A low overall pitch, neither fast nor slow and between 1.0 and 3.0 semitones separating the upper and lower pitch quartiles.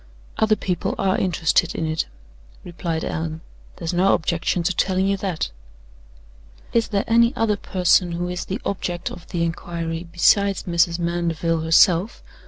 No: medium, 175 Hz; average, 150 wpm; narrow, 2.5 semitones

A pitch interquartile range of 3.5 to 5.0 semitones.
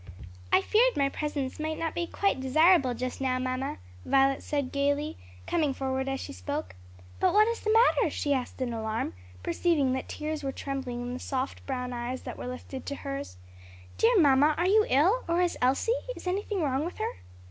Yes: average, 4.2 semitones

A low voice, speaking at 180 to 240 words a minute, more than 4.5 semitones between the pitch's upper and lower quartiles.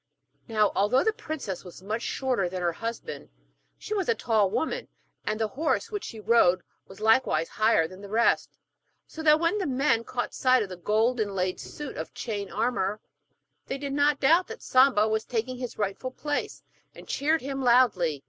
No: high, 230 Hz; average, 185 wpm; average, 5.1 semitones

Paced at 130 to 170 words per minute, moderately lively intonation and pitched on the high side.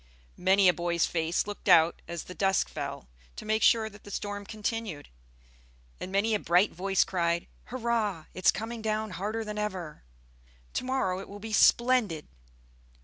Yes: average, 165 wpm; average, 3.5 semitones; high, 200 Hz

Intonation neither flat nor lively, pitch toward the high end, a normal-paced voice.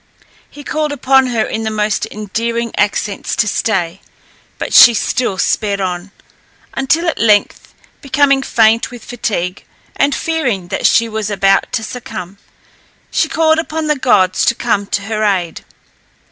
Yes: average, 4.9 semitones; high, 220 Hz; average, 150 wpm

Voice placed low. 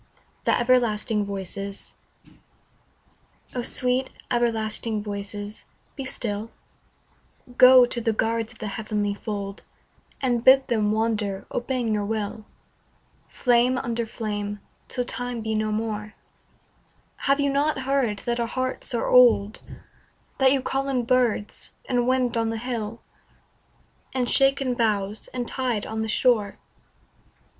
No: high, 230 Hz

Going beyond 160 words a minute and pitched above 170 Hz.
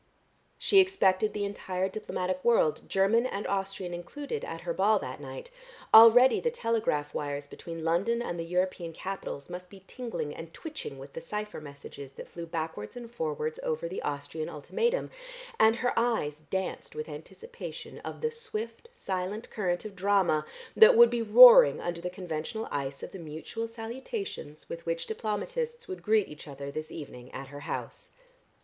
Yes: average, 170 wpm; high, 190 Hz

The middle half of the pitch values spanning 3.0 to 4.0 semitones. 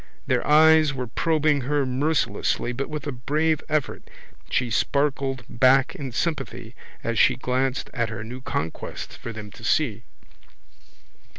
Yes: average, 3.4 semitones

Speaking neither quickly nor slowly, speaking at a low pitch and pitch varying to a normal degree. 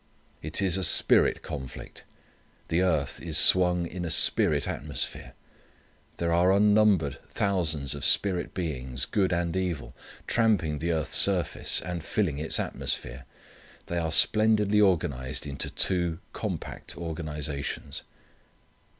No: slow, 125 wpm; very low, 85 Hz; average, 3.7 semitones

